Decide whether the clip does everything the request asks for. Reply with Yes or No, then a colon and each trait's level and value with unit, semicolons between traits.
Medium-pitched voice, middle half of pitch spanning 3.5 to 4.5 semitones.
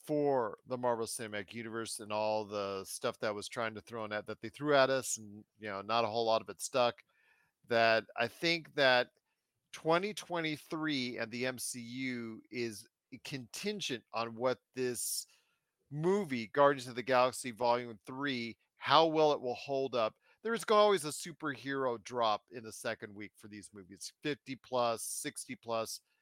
No: low, 120 Hz; average, 3.8 semitones